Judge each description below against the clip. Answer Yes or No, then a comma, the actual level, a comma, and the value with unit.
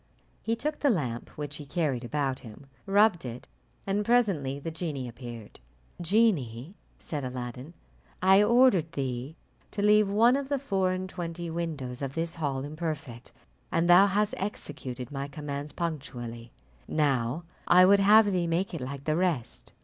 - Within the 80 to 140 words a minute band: No, average, 155 wpm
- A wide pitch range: Yes, wide, 6.5 semitones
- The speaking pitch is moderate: Yes, medium, 160 Hz